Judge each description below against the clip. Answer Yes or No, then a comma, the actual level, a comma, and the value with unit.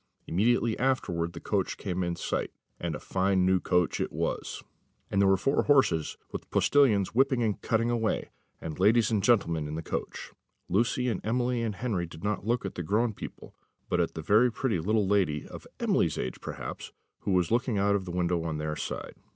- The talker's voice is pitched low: Yes, low, 100 Hz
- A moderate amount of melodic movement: Yes, average, 4.9 semitones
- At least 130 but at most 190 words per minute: No, average, 200 wpm